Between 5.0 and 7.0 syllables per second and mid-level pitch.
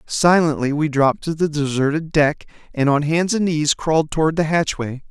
Yes: 5.1 syllables/s; medium, 155 Hz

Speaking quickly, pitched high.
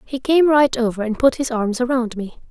Yes: fast, 240 wpm; high, 245 Hz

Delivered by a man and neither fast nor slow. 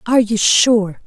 No: female; average, 170 wpm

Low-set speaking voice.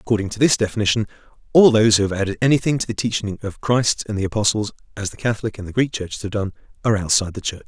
Yes: low, 105 Hz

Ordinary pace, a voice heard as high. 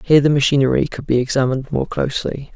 No: average, 190 wpm; low, 135 Hz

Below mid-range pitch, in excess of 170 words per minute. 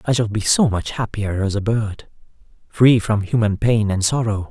Yes: low, 110 Hz; average, 200 wpm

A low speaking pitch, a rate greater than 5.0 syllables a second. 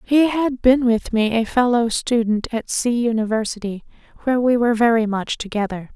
No: high, 230 Hz; 5.2 syllables/s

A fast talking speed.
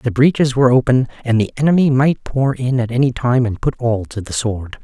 Yes: fast, 235 wpm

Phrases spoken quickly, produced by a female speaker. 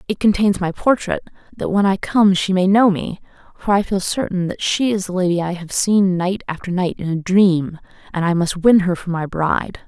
Yes: fast, 230 wpm; female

